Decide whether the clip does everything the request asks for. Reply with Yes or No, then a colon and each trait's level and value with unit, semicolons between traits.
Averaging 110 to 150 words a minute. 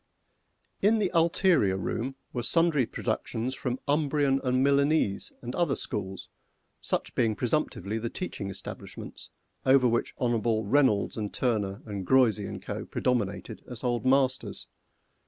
Yes: slow, 135 wpm